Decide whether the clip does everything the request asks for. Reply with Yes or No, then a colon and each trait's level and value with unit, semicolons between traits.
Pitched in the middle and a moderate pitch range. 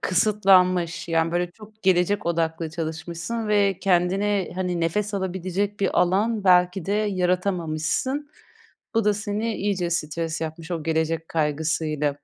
Yes: medium, 180 Hz; average, 3.6 semitones